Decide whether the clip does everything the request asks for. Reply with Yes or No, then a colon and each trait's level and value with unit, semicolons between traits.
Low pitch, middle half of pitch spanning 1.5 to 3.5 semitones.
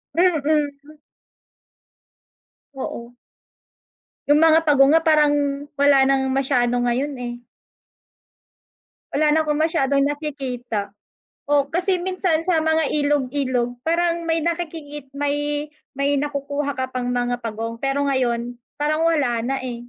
No: very high, 285 Hz; average, 3.1 semitones